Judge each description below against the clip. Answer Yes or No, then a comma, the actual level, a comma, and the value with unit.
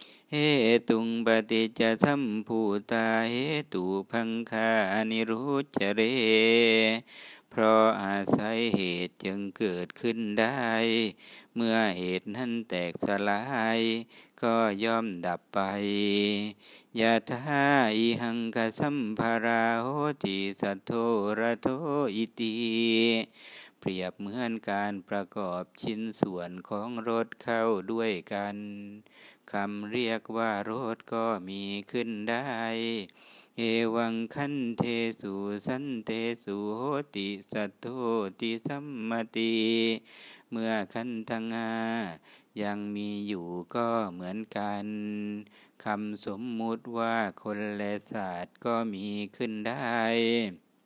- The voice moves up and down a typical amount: No, narrow, 2.0 semitones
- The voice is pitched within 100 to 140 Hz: Yes, low, 115 Hz